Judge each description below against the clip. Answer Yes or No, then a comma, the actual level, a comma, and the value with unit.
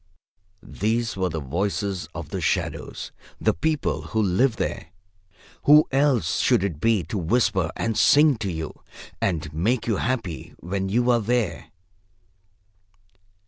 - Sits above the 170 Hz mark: No, low, 105 Hz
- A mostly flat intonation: No, wide, 5.4 semitones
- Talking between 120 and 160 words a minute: Yes, average, 140 wpm